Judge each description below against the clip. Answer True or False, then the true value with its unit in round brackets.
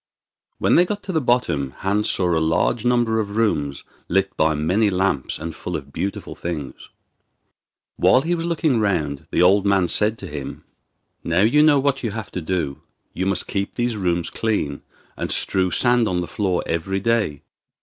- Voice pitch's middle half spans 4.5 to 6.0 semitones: True (5.6 semitones)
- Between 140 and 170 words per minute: False (185 wpm)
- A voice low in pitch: True (95 Hz)